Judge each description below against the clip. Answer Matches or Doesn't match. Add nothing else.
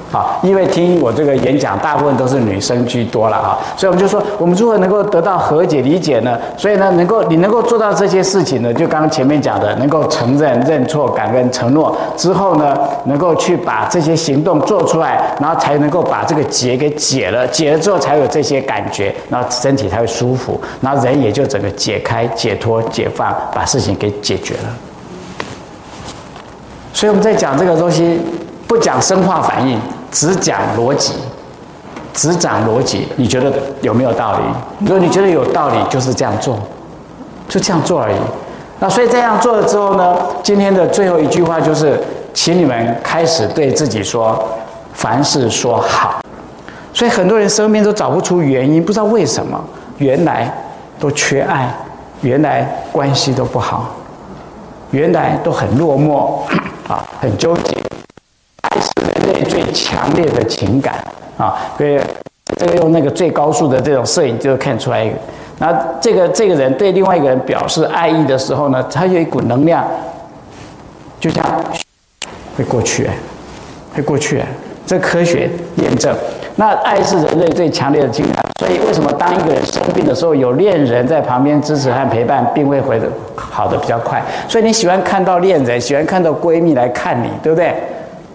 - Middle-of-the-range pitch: Matches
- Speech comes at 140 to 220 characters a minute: Doesn't match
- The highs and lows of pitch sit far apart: Matches